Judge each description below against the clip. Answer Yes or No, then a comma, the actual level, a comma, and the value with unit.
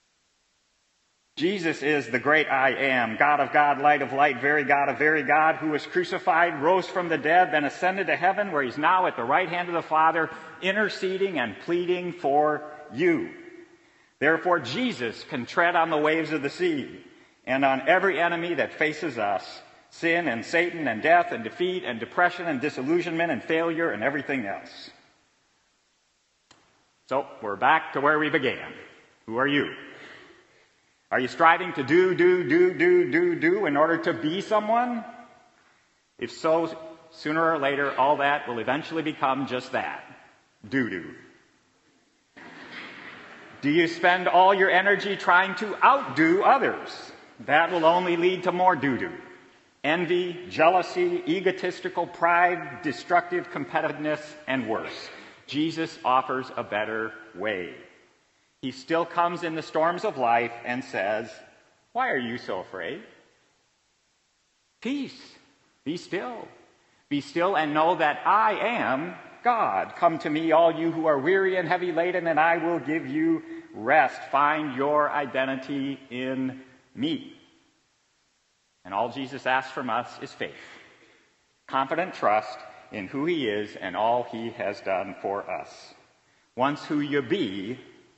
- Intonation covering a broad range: No, average, 4.4 semitones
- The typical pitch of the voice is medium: Yes, medium, 165 Hz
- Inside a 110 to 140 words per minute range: No, average, 150 wpm